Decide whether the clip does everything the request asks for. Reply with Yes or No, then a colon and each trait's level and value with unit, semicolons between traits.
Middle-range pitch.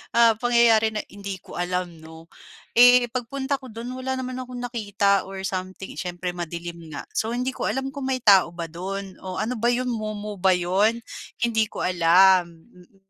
No: high, 205 Hz